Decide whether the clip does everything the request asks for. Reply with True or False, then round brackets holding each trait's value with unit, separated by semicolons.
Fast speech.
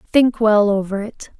False (170 wpm)